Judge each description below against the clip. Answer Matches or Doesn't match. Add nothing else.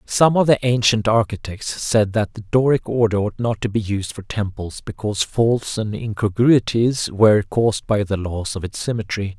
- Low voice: Matches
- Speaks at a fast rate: Doesn't match